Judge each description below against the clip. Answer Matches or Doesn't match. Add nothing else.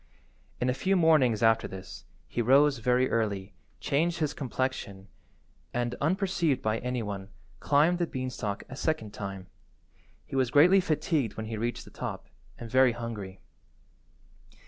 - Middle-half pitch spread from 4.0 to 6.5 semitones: Matches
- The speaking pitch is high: Doesn't match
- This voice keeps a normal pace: Matches